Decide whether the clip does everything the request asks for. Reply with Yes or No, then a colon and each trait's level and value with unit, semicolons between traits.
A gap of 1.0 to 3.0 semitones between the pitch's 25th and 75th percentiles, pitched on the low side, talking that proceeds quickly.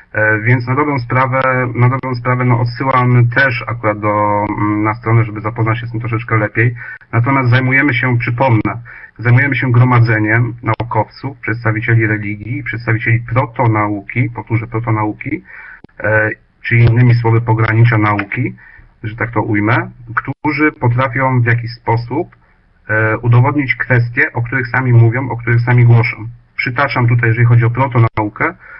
No: narrow, 2.5 semitones; low, 120 Hz; average, 140 wpm